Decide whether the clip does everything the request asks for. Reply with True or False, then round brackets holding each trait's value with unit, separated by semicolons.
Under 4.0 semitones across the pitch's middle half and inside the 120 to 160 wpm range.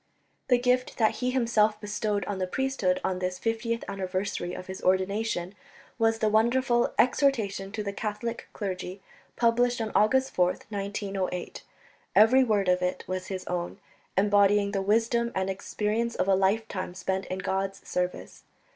True (3.4 semitones; 155 wpm)